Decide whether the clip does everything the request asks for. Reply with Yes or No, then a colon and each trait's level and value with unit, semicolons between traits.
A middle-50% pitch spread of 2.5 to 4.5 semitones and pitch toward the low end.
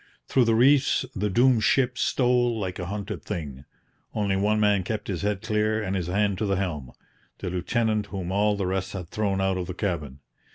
Yes: average, 2.8 semitones; low, 100 Hz